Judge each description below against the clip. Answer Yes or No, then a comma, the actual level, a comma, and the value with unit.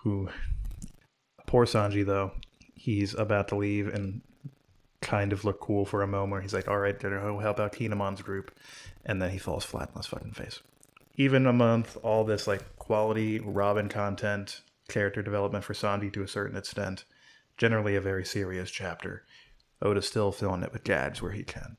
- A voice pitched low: Yes, low, 100 Hz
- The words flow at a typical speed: Yes, average, 180 wpm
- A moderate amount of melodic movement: No, narrow, 1.6 semitones